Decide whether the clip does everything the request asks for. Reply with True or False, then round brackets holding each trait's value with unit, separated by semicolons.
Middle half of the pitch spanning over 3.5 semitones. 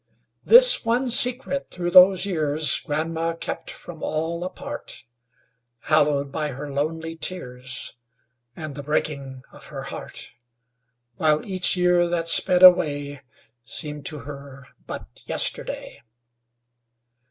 True (3.9 semitones)